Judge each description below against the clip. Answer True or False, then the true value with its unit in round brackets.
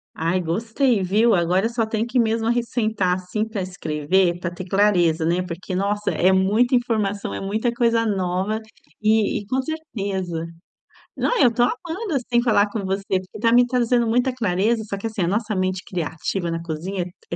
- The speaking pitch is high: True (205 Hz)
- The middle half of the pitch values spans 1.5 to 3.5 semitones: False (4.1 semitones)